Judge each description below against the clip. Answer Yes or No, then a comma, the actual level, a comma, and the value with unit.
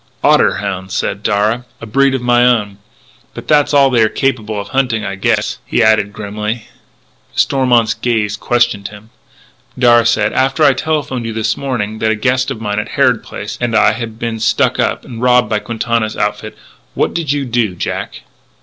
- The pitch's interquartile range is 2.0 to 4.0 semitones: Yes, average, 2.9 semitones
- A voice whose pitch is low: Yes, low, 115 Hz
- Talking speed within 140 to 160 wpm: No, average, 190 wpm